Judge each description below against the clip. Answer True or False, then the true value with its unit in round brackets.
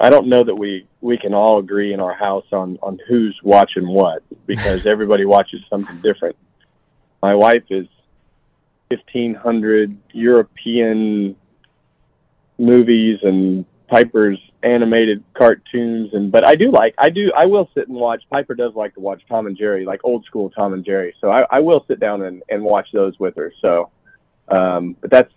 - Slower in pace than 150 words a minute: False (175 wpm)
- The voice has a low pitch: True (105 Hz)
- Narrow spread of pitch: False (3.2 semitones)